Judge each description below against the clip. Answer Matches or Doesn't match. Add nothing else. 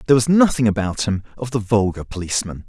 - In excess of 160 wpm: Matches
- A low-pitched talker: Matches